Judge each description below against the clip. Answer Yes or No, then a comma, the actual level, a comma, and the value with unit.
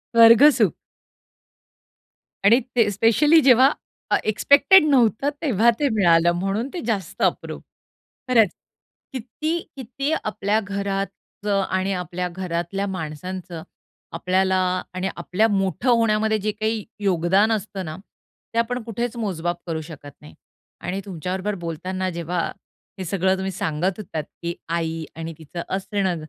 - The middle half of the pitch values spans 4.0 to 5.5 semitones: Yes, average, 4.3 semitones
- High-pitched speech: Yes, high, 195 Hz